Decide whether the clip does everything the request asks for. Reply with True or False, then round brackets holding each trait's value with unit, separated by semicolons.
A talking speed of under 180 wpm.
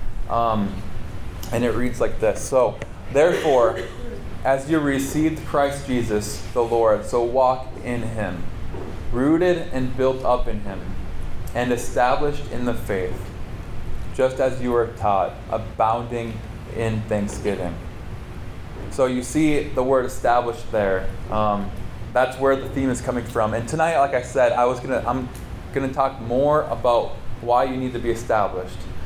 True (150 wpm)